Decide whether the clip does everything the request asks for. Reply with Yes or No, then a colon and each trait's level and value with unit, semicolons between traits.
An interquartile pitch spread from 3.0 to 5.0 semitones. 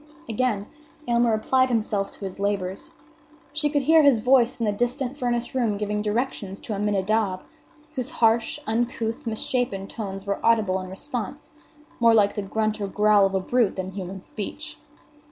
Yes: average, 3.4 semitones